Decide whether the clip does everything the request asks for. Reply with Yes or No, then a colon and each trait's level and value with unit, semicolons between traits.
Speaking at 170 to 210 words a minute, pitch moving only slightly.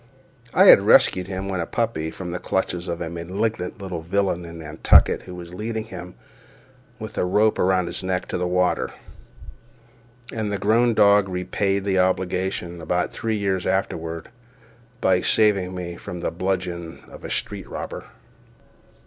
No: average, 160 wpm; narrow, 2.3 semitones